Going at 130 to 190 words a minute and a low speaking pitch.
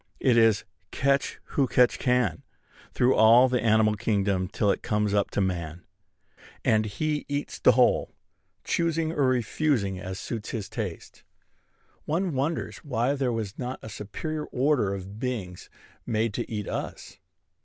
Yes: average, 150 wpm; low, 115 Hz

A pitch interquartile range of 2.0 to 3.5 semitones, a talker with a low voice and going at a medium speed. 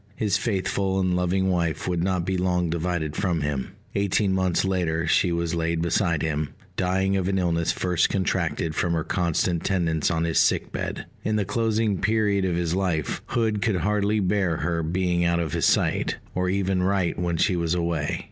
Yes: narrow, 2.4 semitones; very low, 90 Hz; average, 190 wpm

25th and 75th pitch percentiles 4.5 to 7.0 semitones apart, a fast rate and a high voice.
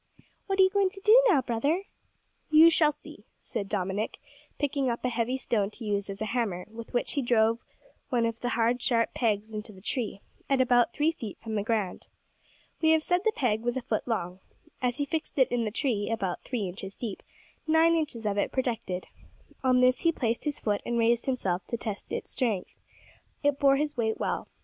Yes: average, 4.8 semitones; fast, 210 wpm; high, 235 Hz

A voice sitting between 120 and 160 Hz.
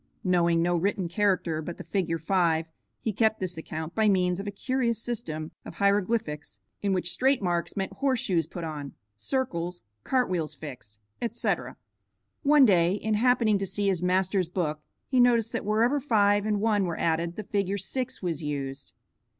No: high, 190 Hz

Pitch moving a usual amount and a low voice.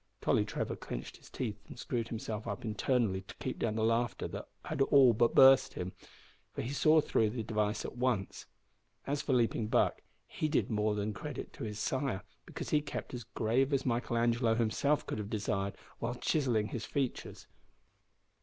Yes: average, 3.3 semitones; low, 115 Hz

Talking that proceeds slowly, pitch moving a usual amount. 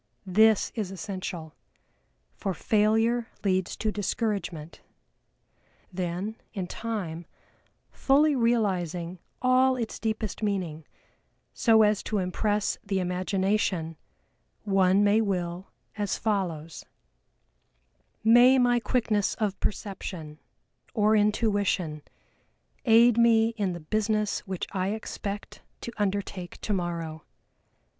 Yes: slow, 100 wpm; average, 3.4 semitones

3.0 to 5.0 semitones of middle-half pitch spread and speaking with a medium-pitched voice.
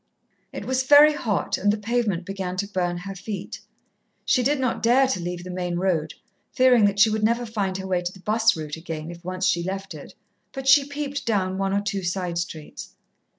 No: average, 4.7 semitones; high, 195 Hz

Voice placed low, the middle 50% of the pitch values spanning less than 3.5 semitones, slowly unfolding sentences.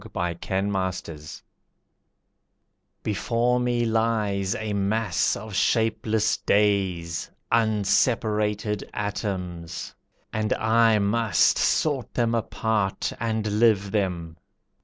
Yes: low, 105 Hz; average, 2.7 semitones; slow, 85 wpm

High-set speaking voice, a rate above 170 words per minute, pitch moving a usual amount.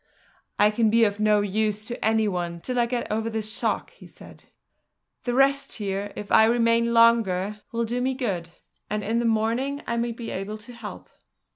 No: high, 225 Hz; average, 195 wpm; narrow, 2.0 semitones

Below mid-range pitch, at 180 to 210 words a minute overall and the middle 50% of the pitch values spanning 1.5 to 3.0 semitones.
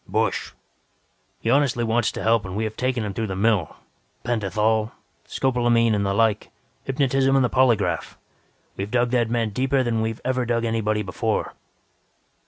No: low, 115 Hz; average, 170 wpm; narrow, 2.6 semitones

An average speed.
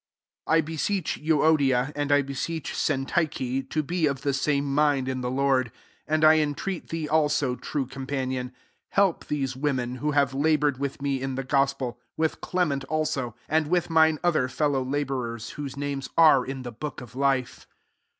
Yes: average, 180 wpm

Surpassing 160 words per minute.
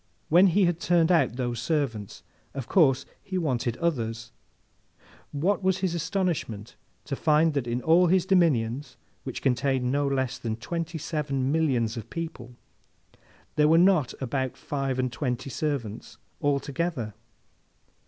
No: average, 140 wpm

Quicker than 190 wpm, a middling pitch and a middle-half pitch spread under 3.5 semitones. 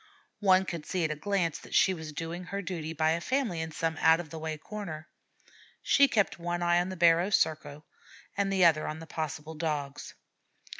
Yes: fast, 205 wpm; medium, 165 Hz; average, 2.9 semitones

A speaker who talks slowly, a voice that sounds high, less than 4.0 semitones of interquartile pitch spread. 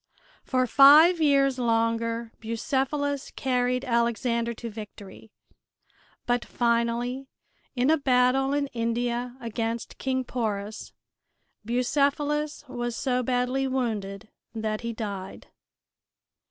Yes: slow, 100 wpm; high, 245 Hz; narrow, 2.6 semitones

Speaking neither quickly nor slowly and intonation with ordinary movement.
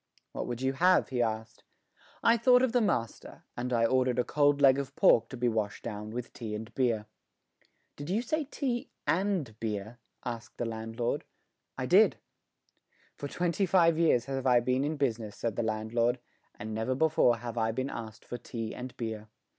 Yes: average, 185 wpm; average, 4.2 semitones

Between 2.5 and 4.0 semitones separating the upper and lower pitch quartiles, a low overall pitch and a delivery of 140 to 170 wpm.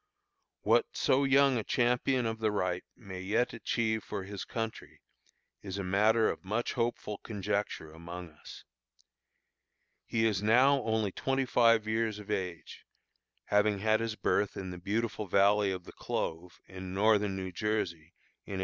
Yes: average, 3.1 semitones; low, 105 Hz; average, 160 wpm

